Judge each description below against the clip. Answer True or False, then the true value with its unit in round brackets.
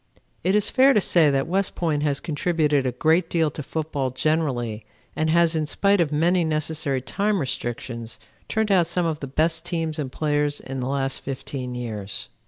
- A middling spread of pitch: True (3.9 semitones)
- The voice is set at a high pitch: False (155 Hz)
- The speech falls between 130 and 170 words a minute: False (190 wpm)